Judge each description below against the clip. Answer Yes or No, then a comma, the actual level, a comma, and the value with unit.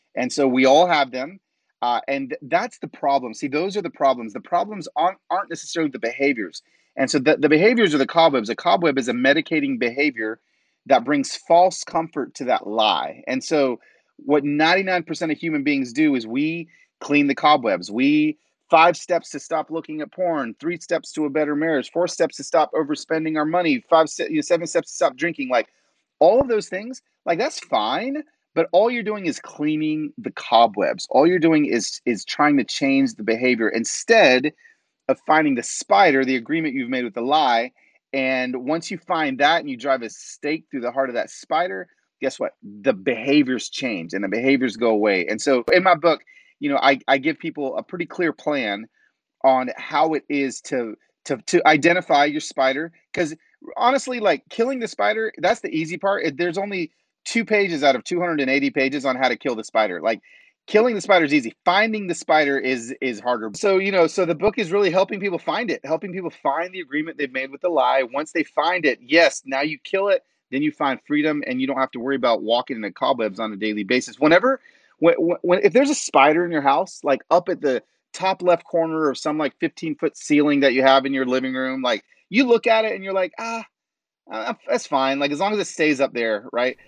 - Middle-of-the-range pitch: Yes, medium, 160 Hz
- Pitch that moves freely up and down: Yes, wide, 6.2 semitones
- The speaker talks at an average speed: No, fast, 215 wpm